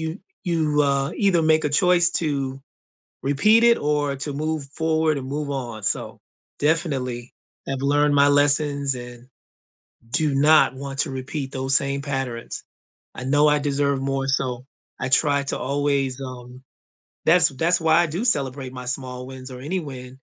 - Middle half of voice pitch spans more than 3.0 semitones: No, average, 2.7 semitones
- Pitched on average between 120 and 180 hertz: Yes, medium, 140 Hz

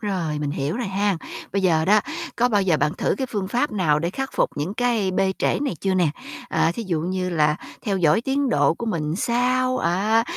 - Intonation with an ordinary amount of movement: No, wide, 5.8 semitones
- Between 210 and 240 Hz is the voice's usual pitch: No, high, 190 Hz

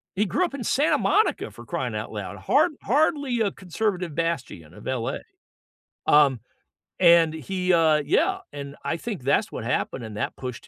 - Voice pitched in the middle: Yes, medium, 170 Hz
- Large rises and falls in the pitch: Yes, wide, 7.8 semitones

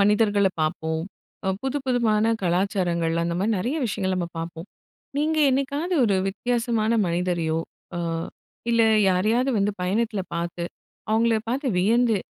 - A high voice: Yes, high, 205 Hz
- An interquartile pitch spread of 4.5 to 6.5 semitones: Yes, average, 5.1 semitones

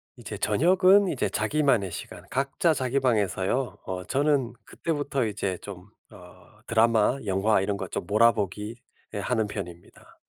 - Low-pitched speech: Yes, low, 110 Hz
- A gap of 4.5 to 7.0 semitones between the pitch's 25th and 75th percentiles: Yes, wide, 5.4 semitones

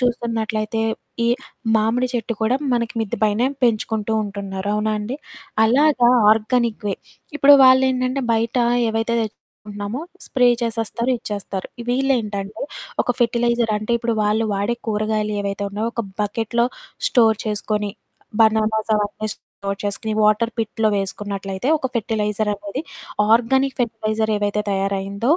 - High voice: Yes, high, 220 Hz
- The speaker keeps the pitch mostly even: Yes, narrow, 2.2 semitones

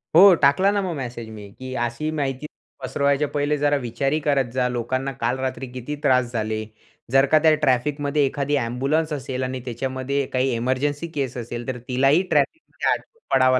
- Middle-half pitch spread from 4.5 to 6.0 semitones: No, average, 2.7 semitones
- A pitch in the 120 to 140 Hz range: Yes, low, 135 Hz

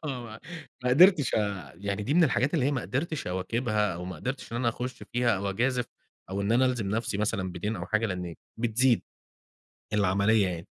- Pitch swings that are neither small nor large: Yes, average, 4.4 semitones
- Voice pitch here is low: Yes, low, 110 Hz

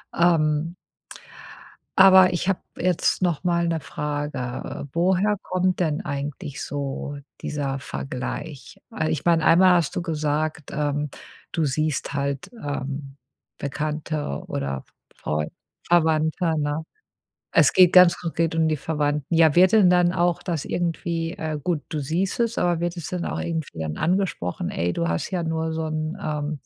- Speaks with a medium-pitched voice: Yes, medium, 160 Hz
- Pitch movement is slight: No, average, 3.1 semitones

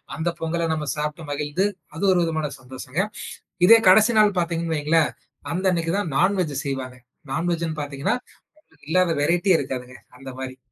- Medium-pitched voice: Yes, medium, 160 Hz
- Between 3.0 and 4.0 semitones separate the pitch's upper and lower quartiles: Yes, average, 3.6 semitones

